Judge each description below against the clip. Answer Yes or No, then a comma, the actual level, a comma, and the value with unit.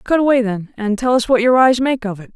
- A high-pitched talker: Yes, high, 235 Hz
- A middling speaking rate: No, fast, 305 wpm